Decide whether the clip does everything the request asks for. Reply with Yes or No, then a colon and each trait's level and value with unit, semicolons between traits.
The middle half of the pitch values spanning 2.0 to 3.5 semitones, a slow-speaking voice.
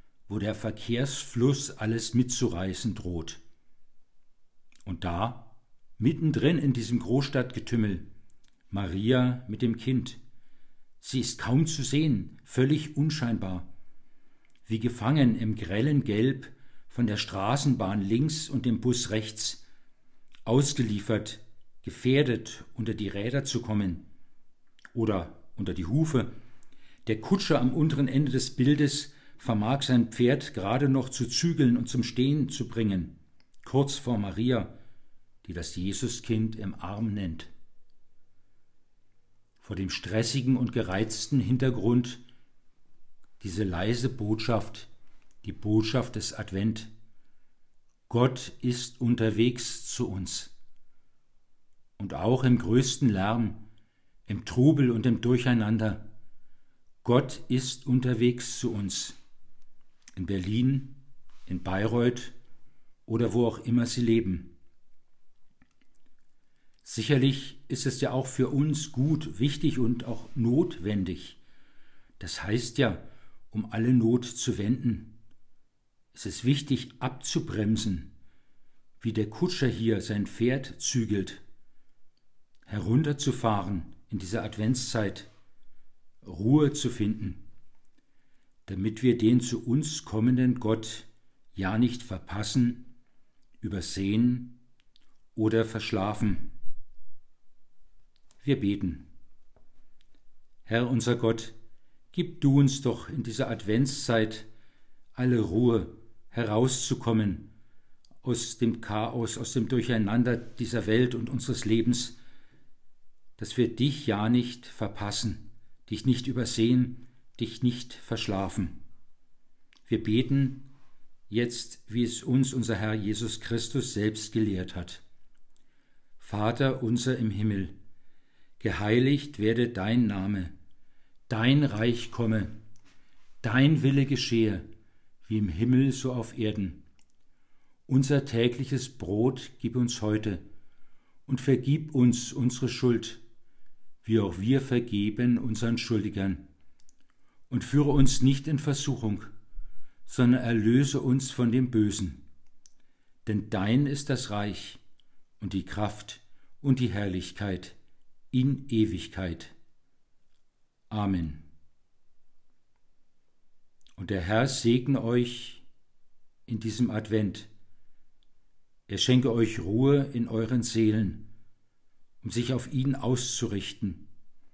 Yes: average, 3.2 semitones; slow, 105 wpm